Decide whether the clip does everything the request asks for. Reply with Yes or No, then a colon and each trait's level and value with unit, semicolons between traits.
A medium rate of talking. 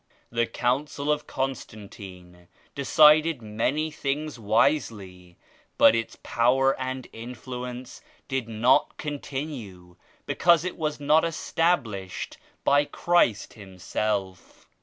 No: slow, 100 wpm